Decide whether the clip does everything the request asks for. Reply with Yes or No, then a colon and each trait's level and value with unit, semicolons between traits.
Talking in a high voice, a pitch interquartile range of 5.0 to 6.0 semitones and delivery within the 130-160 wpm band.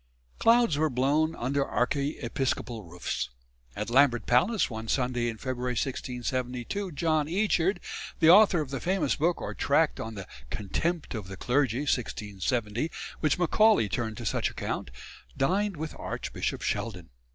No: low, 135 Hz; wide, 5.4 semitones; average, 140 wpm